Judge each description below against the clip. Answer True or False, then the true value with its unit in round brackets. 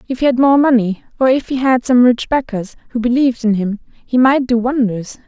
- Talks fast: True (230 wpm)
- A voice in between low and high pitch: False (245 Hz)